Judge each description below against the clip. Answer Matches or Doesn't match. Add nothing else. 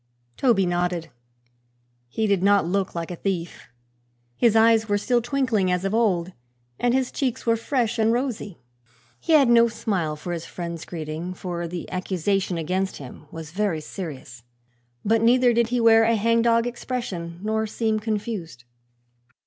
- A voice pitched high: Matches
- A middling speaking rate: Matches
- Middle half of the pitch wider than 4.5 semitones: Matches